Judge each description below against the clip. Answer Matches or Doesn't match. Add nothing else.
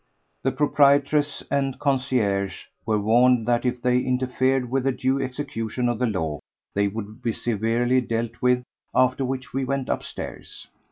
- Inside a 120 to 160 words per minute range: Matches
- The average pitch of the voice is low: Matches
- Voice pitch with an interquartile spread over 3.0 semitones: Doesn't match